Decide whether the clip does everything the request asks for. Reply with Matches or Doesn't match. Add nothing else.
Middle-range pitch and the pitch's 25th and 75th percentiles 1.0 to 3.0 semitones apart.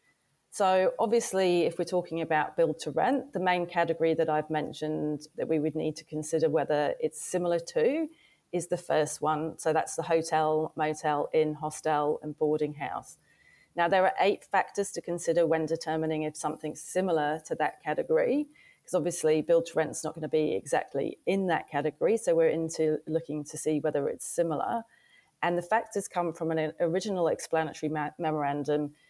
Matches